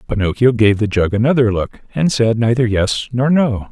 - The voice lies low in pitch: Yes, low, 115 Hz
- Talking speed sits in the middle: Yes, average, 195 wpm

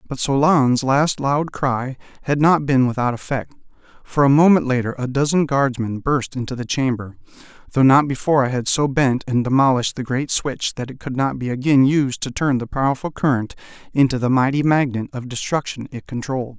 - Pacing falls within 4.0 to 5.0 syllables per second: No, 5.4 syllables/s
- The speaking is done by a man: Yes, male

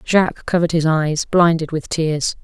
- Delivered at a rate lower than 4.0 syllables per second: No, 4.8 syllables/s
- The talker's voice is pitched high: No, medium, 160 Hz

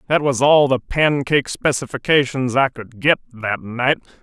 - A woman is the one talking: No, male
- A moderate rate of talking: Yes, average, 155 wpm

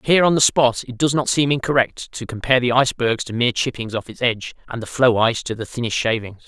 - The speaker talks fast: Yes, fast, 250 wpm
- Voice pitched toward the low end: Yes, low, 125 Hz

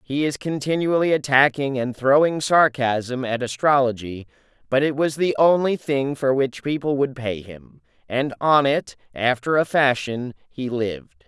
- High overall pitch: No, low, 135 Hz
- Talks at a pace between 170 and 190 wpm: No, average, 155 wpm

